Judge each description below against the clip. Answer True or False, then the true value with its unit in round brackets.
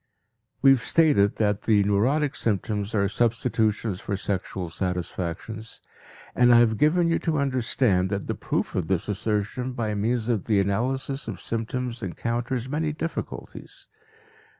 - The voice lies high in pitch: False (110 Hz)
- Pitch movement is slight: False (4.1 semitones)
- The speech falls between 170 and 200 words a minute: False (145 wpm)